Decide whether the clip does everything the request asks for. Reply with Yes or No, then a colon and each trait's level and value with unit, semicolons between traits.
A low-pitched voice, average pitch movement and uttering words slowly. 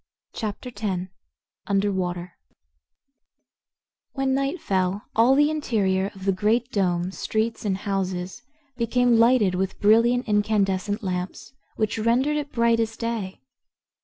No: high, 210 Hz; average, 3.8 semitones; slow, 125 wpm